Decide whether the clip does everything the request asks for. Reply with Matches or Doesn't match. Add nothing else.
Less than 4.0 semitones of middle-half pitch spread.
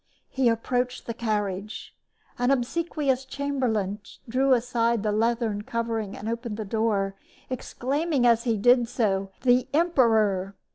Matches